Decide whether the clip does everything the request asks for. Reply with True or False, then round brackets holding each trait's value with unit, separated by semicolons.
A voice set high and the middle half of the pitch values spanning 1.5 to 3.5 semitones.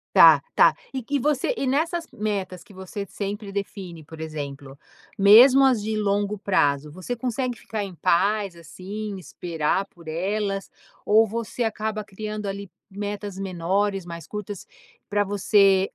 True (200 Hz; 2.6 semitones)